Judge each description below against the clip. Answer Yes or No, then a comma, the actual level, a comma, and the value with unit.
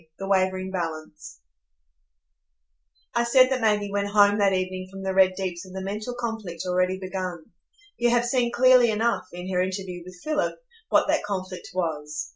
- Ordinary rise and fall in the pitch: Yes, average, 3.2 semitones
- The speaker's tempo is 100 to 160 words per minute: No, average, 170 wpm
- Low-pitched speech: No, high, 190 Hz